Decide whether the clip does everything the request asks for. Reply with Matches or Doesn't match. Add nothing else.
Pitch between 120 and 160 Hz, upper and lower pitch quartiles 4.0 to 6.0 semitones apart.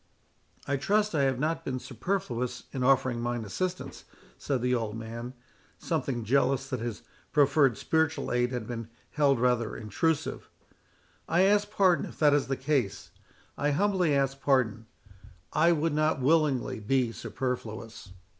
Matches